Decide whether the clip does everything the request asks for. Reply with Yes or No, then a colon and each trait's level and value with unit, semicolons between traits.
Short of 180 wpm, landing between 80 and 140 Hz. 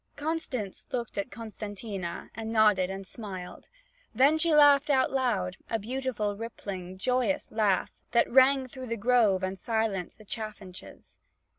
No: average, 140 wpm; high, 225 Hz